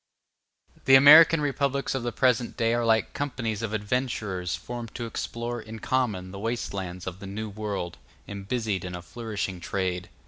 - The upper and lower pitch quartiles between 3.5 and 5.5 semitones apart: Yes, average, 3.9 semitones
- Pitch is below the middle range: Yes, low, 110 Hz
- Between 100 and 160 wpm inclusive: No, average, 175 wpm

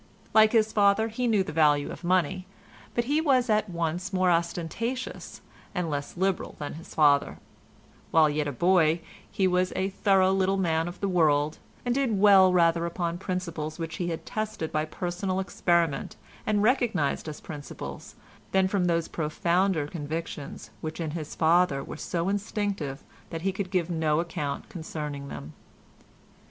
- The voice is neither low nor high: Yes, medium, 175 Hz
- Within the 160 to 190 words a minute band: Yes, average, 165 wpm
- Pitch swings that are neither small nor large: Yes, average, 3.6 semitones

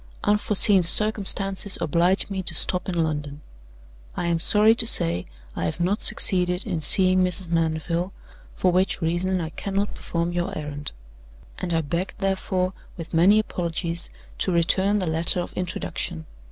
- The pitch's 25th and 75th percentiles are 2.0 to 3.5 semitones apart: Yes, narrow, 2.6 semitones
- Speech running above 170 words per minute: No, average, 155 wpm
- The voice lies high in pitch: No, medium, 180 Hz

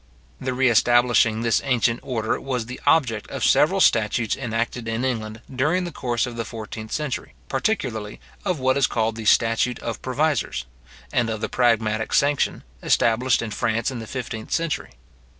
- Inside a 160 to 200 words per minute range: Yes, average, 170 wpm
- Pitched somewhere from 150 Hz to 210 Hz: No, low, 120 Hz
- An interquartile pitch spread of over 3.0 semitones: No, average, 2.7 semitones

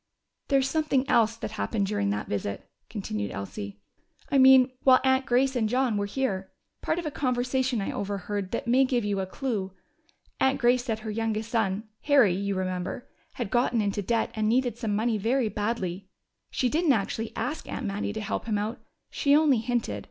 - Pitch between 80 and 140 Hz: No, high, 225 Hz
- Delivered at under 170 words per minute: No, average, 190 wpm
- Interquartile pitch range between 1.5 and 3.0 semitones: No, average, 4.2 semitones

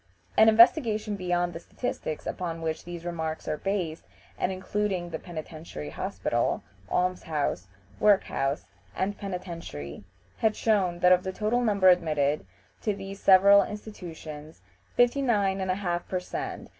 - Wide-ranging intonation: No, average, 3.8 semitones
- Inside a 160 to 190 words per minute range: No, average, 140 wpm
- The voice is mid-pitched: Yes, medium, 180 Hz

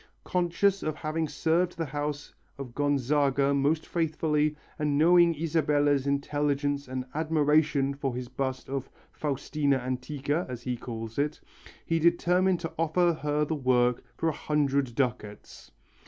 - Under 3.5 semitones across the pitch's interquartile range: Yes, average, 2.7 semitones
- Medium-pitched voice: Yes, medium, 145 Hz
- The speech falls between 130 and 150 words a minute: Yes, average, 140 wpm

